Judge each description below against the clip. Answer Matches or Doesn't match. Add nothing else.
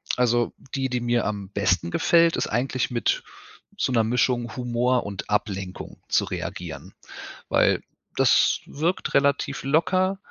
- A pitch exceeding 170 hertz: Doesn't match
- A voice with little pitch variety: Doesn't match